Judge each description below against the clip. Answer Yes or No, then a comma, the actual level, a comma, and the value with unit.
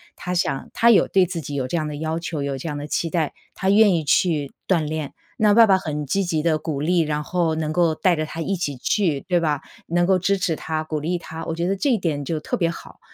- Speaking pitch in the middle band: Yes, medium, 165 Hz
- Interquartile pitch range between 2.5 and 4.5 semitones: Yes, average, 3.0 semitones